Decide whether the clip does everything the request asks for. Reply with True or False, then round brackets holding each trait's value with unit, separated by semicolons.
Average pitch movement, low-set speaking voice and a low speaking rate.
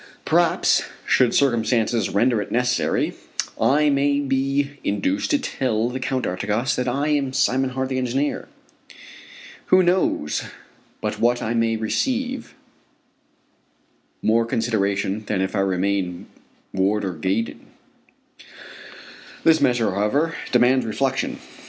True (4.4 semitones; 125 Hz; 115 wpm)